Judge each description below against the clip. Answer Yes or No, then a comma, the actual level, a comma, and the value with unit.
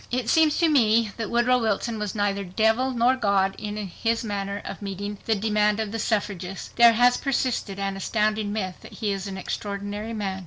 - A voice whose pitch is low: No, high, 210 Hz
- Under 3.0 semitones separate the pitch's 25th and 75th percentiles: Yes, narrow, 2.5 semitones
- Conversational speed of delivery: Yes, average, 195 wpm